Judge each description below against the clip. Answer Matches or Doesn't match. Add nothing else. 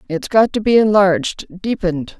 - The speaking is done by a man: Doesn't match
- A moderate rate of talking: Matches